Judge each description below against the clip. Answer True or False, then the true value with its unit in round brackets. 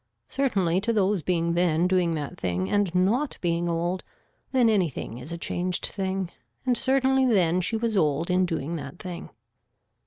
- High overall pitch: False (180 Hz)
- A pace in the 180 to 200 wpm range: False (165 wpm)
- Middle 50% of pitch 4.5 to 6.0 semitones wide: False (3.6 semitones)